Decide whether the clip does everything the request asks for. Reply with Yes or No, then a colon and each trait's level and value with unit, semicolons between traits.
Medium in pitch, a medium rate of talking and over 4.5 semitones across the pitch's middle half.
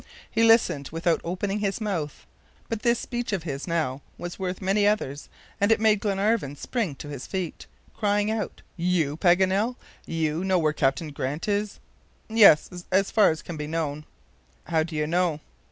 Yes: medium, 180 Hz; average, 170 wpm; average, 5.0 semitones